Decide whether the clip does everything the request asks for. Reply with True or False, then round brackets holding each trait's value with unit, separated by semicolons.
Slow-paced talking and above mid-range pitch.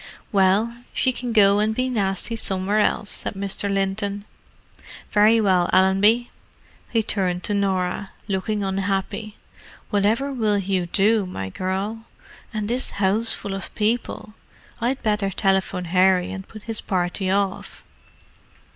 True (130 wpm; 200 Hz)